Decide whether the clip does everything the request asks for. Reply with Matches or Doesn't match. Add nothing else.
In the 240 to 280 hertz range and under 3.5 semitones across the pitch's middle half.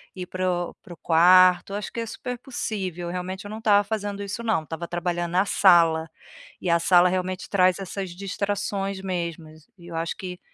Doesn't match